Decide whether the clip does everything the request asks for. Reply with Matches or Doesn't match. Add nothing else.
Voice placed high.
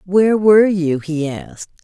Doesn't match